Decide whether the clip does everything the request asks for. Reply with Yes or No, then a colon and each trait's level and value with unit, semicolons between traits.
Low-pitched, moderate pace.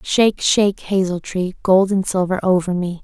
No: high, 190 Hz; average, 180 wpm